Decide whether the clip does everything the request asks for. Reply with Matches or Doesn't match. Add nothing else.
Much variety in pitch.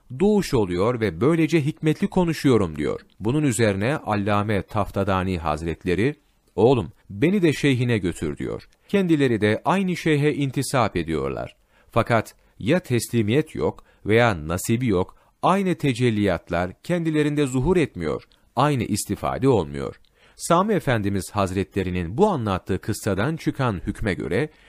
Matches